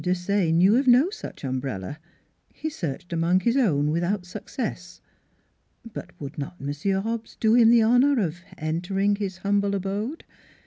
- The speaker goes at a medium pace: Yes, average, 150 wpm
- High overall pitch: Yes, high, 195 Hz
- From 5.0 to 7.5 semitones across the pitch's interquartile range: Yes, average, 5.3 semitones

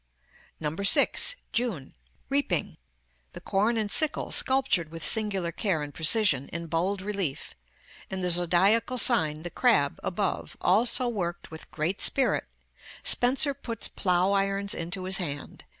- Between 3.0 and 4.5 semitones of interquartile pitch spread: No, average, 5.1 semitones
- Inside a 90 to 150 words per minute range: Yes, slow, 135 wpm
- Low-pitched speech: No, high, 195 Hz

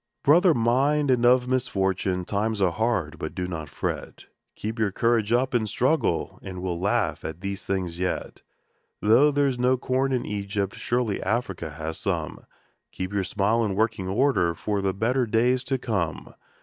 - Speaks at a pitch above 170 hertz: No, low, 110 Hz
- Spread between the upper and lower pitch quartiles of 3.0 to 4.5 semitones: No, average, 4.9 semitones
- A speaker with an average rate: Yes, average, 175 wpm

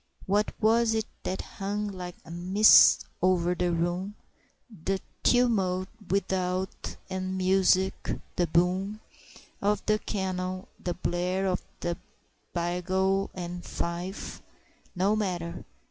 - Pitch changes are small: Yes, narrow, 1.8 semitones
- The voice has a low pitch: No, medium, 185 Hz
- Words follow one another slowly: Yes, slow, 115 wpm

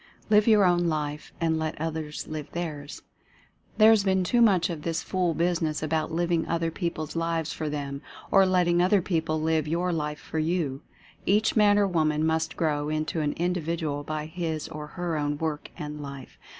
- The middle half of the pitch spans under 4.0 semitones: Yes, narrow, 2.4 semitones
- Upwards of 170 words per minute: Yes, average, 185 wpm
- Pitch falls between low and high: Yes, medium, 160 Hz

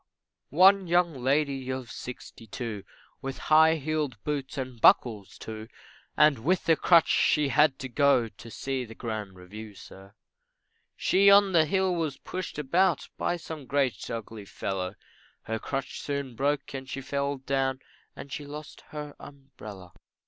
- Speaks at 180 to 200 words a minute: No, average, 155 wpm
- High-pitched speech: No, low, 135 Hz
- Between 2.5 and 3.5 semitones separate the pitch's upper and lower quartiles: No, average, 4.7 semitones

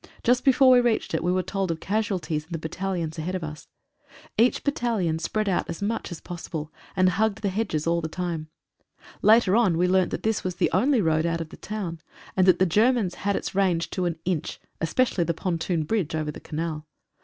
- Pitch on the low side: No, medium, 180 Hz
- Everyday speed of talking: No, fast, 215 wpm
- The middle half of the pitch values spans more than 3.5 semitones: Yes, average, 4.4 semitones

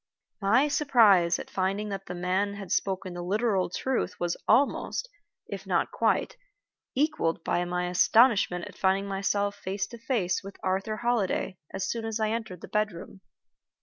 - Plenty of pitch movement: No, average, 3.3 semitones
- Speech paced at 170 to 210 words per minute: No, average, 160 wpm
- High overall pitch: Yes, high, 195 Hz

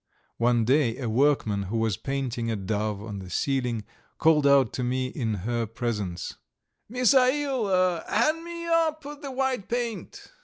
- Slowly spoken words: No, average, 150 wpm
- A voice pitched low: Yes, low, 130 Hz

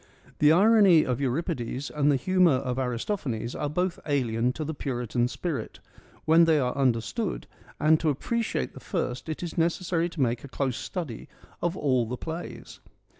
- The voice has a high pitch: No, medium, 145 Hz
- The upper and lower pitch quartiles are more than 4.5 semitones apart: Yes, average, 5.2 semitones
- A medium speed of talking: Yes, average, 170 wpm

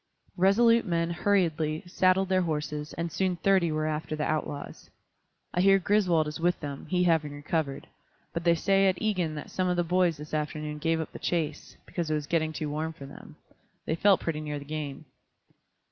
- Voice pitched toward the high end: No, medium, 165 Hz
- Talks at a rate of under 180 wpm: No, average, 195 wpm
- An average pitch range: Yes, average, 3.1 semitones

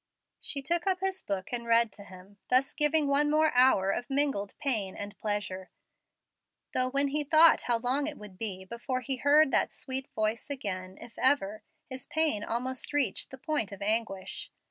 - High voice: Yes, very high, 250 Hz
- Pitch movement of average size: No, wide, 5.7 semitones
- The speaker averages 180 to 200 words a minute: Yes, average, 185 wpm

